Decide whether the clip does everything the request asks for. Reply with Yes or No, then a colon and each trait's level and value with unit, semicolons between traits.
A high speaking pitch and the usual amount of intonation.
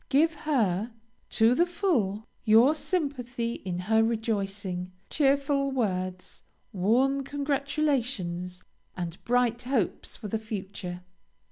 No: high, 230 Hz; wide, 6.3 semitones